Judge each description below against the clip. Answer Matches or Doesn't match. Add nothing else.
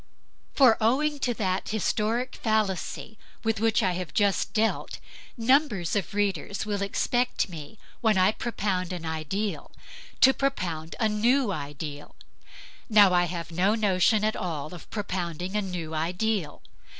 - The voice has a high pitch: Matches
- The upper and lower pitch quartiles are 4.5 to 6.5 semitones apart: Doesn't match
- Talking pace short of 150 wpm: Matches